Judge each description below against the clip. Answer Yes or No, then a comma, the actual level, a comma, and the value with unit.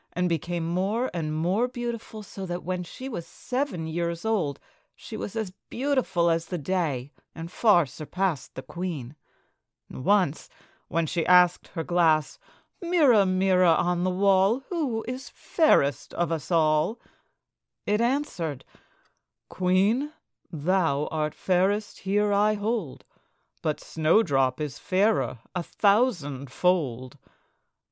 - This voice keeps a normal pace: No, slow, 125 wpm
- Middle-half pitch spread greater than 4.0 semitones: Yes, average, 4.9 semitones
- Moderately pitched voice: Yes, medium, 180 Hz